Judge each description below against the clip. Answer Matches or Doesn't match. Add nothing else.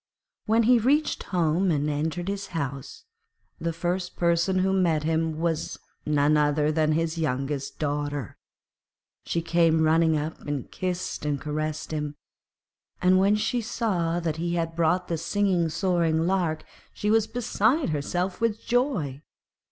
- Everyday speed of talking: Matches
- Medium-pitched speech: Matches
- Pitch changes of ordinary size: Matches